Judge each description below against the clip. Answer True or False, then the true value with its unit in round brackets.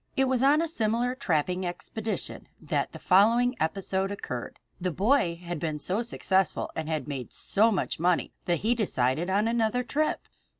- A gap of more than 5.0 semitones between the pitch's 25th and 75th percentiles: True (5.6 semitones)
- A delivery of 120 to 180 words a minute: True (170 wpm)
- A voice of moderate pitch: False (195 Hz)